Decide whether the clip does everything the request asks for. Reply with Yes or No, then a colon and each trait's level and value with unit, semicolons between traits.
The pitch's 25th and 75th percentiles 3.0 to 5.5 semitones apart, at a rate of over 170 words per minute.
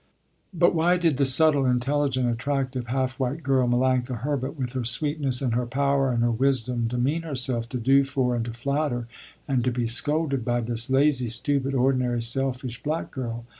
No: narrow, 2.4 semitones; average, 180 wpm